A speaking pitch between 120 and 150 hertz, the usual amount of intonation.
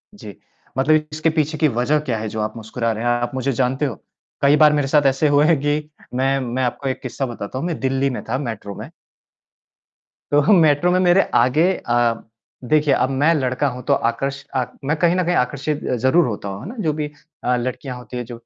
Yes: low, 135 Hz; average, 3.6 semitones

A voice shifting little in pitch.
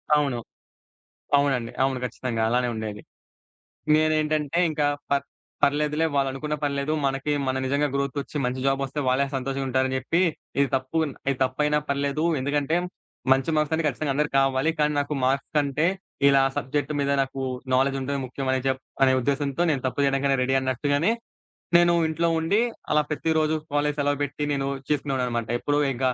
Yes: narrow, 2.1 semitones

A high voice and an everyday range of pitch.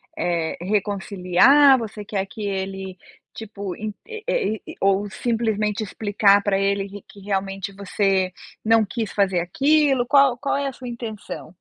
Yes: high, 205 Hz; average, 3.3 semitones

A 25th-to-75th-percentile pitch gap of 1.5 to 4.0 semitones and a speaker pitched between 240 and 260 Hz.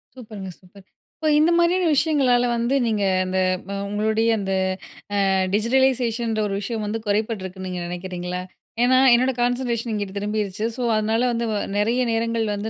No: average, 3.3 semitones; high, 220 Hz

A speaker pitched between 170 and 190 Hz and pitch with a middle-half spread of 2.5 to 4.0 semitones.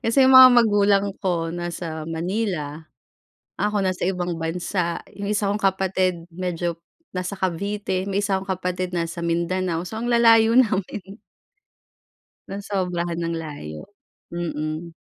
Yes: medium, 185 Hz; average, 2.9 semitones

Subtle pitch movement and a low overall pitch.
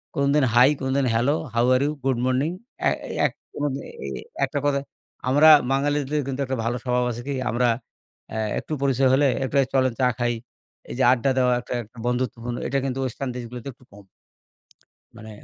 Yes: narrow, 2.2 semitones; low, 130 Hz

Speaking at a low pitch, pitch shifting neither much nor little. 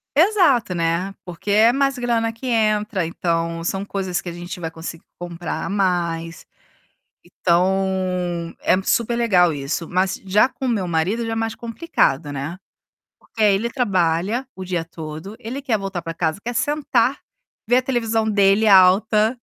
No: high, 195 Hz; average, 4.8 semitones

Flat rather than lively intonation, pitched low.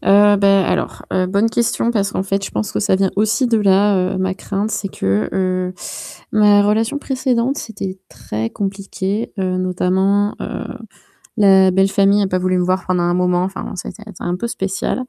No: narrow, 2.1 semitones; high, 195 Hz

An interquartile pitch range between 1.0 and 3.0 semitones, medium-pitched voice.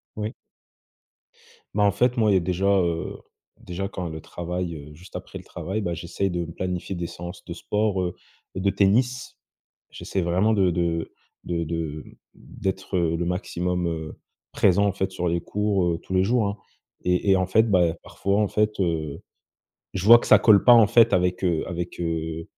No: average, 2.7 semitones; very low, 90 Hz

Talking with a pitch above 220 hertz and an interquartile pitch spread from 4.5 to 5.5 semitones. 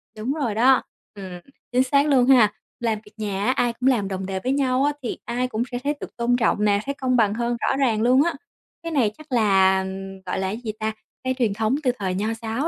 No: high, 235 Hz; average, 3.7 semitones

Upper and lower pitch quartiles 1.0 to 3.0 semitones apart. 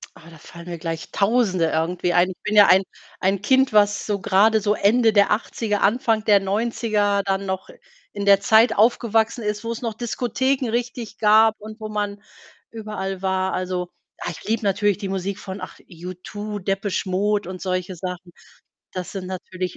Yes: average, 2.7 semitones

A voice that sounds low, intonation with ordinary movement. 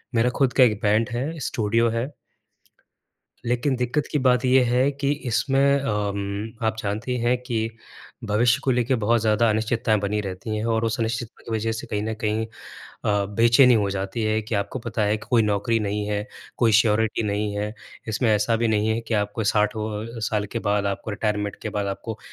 No: low, 110 Hz; narrow, 2.2 semitones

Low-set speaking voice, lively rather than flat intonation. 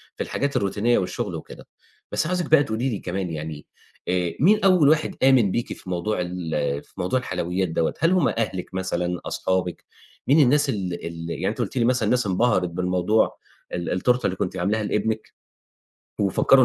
Yes: low, 100 Hz; wide, 6.1 semitones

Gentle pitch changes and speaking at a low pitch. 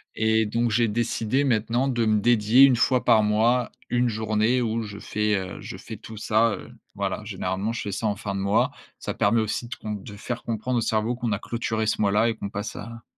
Yes: narrow, 1.9 semitones; low, 110 Hz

